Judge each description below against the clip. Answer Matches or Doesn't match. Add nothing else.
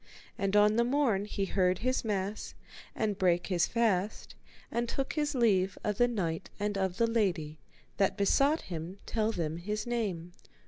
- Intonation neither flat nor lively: Matches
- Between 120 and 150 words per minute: Doesn't match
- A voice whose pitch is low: Doesn't match